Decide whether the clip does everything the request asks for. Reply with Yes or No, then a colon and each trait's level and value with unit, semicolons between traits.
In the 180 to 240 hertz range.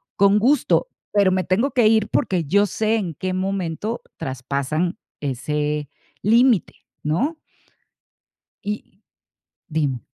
Yes: medium, 185 Hz